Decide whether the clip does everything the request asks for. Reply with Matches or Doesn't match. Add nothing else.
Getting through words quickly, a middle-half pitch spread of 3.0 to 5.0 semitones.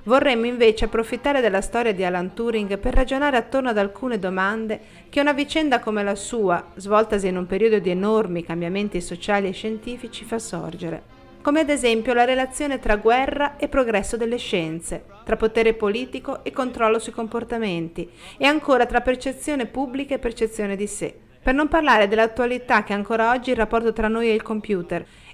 Matches